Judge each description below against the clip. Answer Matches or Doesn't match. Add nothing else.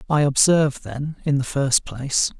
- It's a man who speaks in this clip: Matches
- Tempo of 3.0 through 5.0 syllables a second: Matches